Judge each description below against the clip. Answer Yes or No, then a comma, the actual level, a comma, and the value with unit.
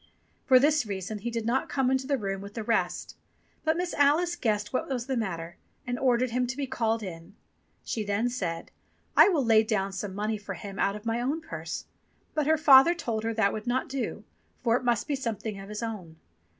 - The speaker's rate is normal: No, fast, 220 wpm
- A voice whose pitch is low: No, high, 230 Hz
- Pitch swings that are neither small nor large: Yes, average, 4.3 semitones